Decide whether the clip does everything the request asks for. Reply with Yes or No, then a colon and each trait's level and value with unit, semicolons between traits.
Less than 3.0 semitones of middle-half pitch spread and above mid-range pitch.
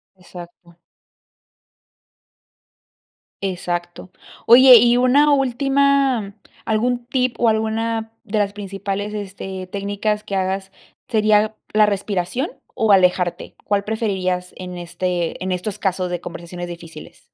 No: average, 3.6 semitones; high, 200 Hz